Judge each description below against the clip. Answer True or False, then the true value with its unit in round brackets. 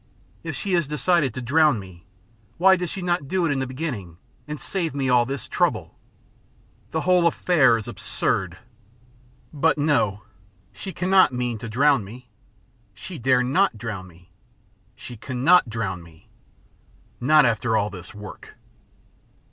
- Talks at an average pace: True (150 wpm)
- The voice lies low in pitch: True (130 Hz)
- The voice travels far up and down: True (7.0 semitones)